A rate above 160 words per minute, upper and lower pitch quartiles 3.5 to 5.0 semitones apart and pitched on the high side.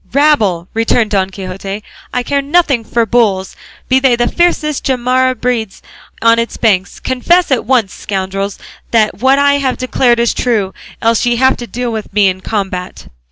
Yes: average, 170 wpm; average, 4.5 semitones; high, 235 Hz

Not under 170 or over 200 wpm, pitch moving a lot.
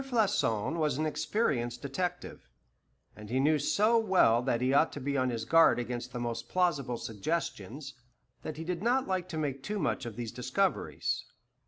Yes: average, 180 wpm; wide, 6.8 semitones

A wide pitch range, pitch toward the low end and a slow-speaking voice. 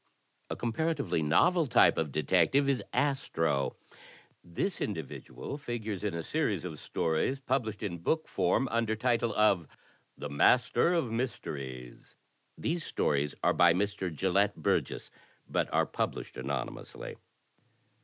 Yes: wide, 8.2 semitones; low, 105 Hz; slow, 125 wpm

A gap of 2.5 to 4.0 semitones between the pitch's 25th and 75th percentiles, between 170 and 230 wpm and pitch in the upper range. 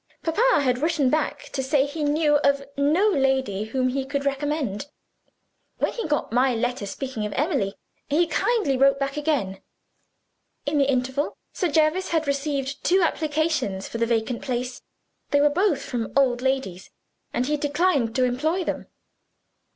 No: average, 3.4 semitones; average, 160 wpm; very high, 280 Hz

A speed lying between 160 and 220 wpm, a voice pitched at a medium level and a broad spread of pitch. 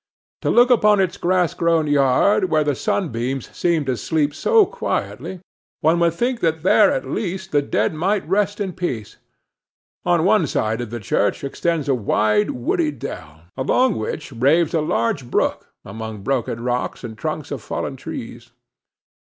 Yes: average, 165 wpm; medium, 150 Hz; wide, 6.8 semitones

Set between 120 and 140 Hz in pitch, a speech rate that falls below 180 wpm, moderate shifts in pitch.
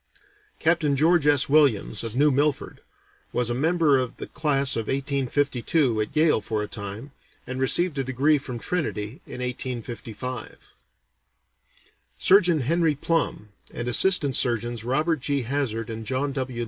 Yes: low, 135 Hz; average, 145 wpm; average, 4.0 semitones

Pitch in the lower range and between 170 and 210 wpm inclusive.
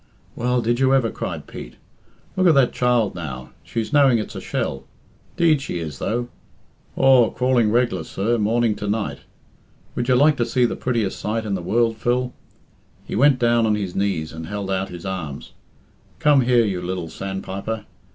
Yes: low, 115 Hz; average, 180 wpm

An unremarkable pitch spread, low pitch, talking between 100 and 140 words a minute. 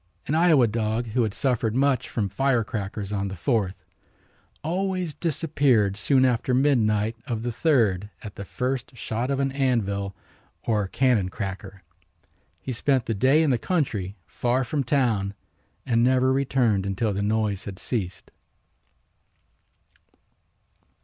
Yes: average, 4.7 semitones; low, 115 Hz; slow, 135 wpm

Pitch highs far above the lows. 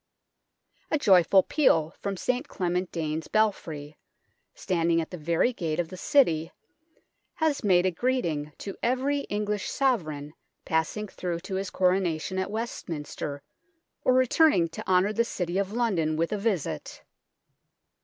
No: average, 4.9 semitones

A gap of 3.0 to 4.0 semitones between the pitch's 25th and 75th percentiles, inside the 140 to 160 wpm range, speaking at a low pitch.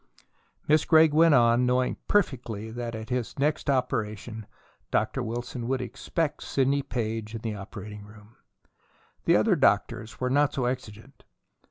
Yes: average, 3.5 semitones; average, 145 wpm; low, 120 Hz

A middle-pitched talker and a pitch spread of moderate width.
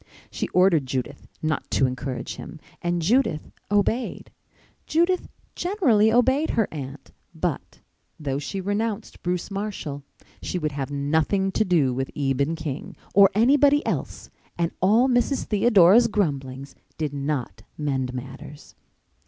No: medium, 175 Hz; wide, 7.4 semitones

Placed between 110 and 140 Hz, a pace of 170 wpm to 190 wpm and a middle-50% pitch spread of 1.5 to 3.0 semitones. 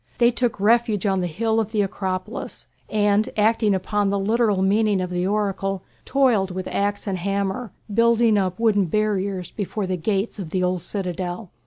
No: high, 200 Hz; average, 175 wpm; average, 2.7 semitones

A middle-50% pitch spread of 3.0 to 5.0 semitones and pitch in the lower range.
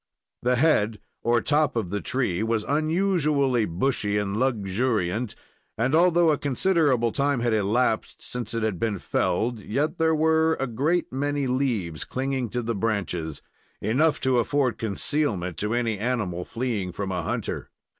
No: wide, 5.4 semitones; low, 120 Hz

